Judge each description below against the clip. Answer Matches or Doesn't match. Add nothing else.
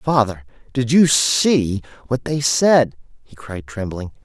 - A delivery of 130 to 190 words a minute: Matches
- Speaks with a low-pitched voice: Matches